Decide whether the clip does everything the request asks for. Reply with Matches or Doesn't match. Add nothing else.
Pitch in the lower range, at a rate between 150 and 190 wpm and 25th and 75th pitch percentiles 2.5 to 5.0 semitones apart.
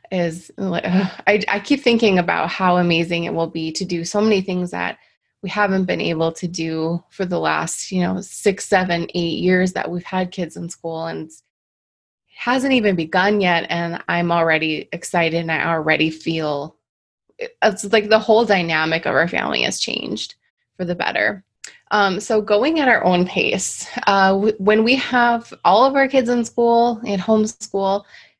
Doesn't match